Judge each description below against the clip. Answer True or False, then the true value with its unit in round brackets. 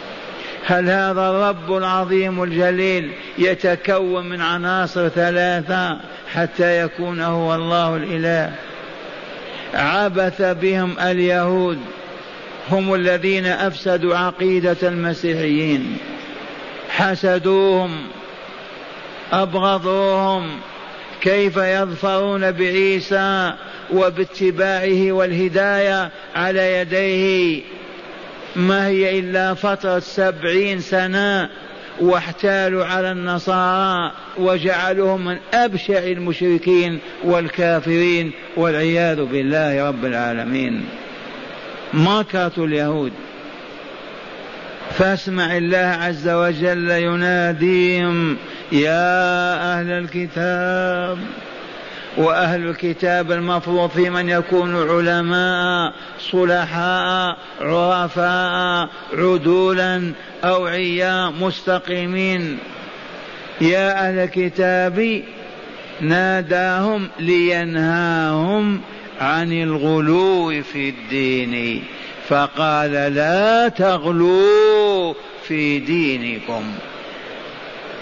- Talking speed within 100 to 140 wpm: False (65 wpm)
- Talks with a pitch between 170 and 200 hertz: True (180 Hz)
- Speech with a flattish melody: True (1.7 semitones)